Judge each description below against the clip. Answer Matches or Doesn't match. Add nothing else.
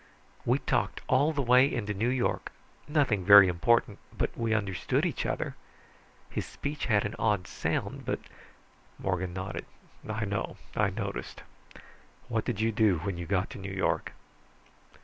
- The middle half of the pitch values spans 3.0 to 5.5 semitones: Matches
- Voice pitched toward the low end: Matches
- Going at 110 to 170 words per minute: Matches